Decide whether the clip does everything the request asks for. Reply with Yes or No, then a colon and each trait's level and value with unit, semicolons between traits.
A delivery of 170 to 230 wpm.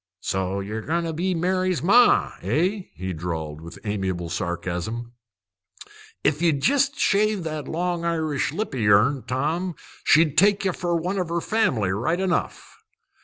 No: average, 150 wpm